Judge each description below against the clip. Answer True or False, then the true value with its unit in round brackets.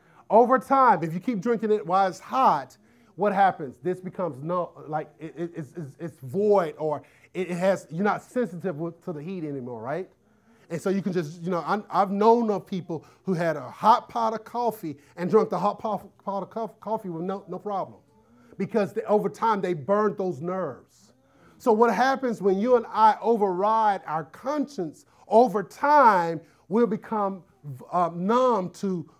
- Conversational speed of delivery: True (180 wpm)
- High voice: True (195 Hz)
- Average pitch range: True (4.5 semitones)